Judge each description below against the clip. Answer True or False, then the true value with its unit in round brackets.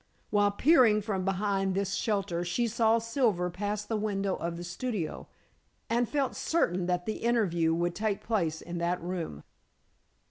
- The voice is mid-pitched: False (200 Hz)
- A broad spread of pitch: False (4.0 semitones)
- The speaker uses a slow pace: False (155 wpm)